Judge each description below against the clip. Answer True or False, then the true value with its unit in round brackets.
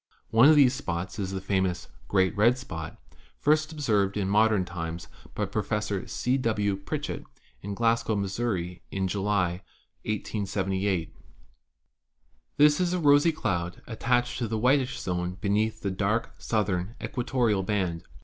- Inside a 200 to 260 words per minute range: False (140 wpm)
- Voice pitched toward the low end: True (105 Hz)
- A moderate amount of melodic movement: True (4.1 semitones)